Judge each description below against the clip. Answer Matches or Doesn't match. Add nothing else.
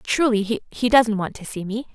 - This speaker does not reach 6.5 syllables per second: Matches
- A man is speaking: Doesn't match